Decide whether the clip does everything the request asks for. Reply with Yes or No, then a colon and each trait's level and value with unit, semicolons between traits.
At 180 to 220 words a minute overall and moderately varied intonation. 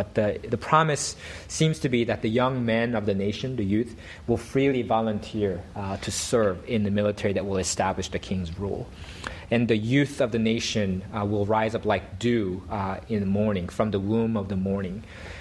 Yes: fast, 205 wpm; average, 3.1 semitones